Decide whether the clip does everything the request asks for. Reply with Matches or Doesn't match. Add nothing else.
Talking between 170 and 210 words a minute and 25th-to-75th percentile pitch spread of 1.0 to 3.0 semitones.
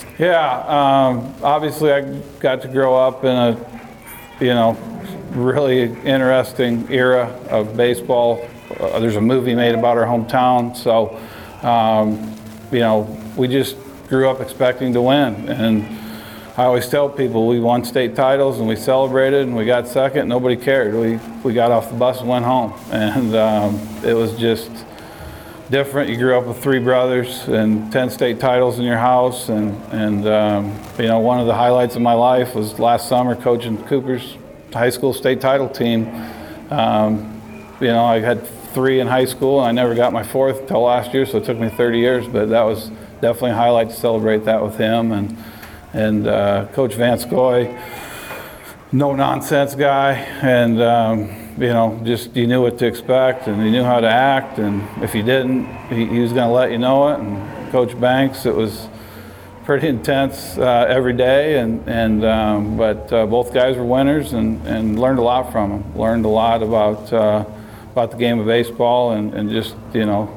Matches